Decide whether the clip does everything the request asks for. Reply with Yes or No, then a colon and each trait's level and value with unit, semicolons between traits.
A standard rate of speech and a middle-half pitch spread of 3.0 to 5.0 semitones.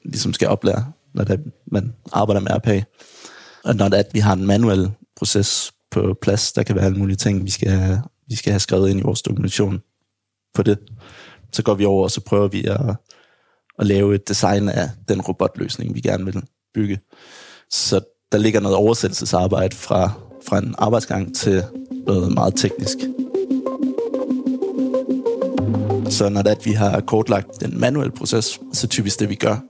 Yes: average, 180 wpm; average, 3.3 semitones